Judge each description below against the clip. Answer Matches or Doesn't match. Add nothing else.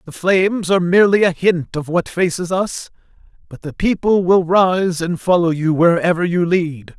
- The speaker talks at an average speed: Matches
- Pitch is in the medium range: Matches